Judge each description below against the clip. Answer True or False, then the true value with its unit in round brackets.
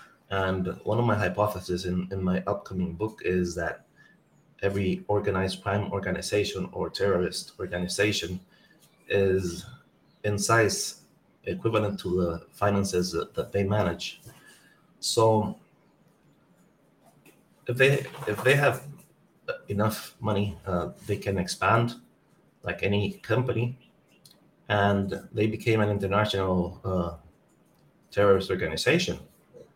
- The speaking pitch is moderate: False (100 Hz)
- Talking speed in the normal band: False (105 wpm)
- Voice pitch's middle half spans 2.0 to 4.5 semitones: True (2.6 semitones)